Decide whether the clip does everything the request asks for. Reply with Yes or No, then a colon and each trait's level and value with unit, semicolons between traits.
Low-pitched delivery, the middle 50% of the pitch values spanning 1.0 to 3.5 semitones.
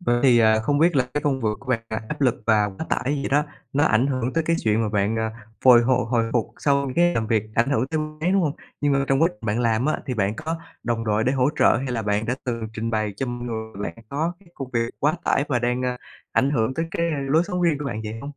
No: low, 125 Hz; average, 4.4 semitones